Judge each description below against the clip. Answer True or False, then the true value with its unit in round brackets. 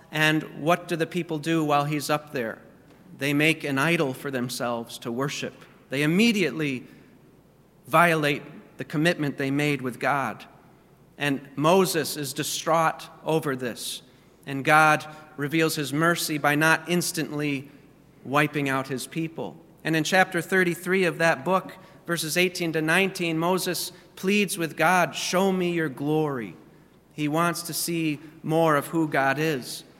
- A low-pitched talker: False (155 Hz)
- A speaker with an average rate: True (145 wpm)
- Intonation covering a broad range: False (2.9 semitones)